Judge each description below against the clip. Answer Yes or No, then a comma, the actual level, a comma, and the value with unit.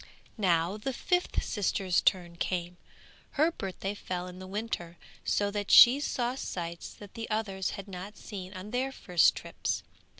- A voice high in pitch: Yes, high, 195 Hz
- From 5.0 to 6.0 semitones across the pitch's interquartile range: No, average, 3.7 semitones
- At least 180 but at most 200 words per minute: No, average, 160 wpm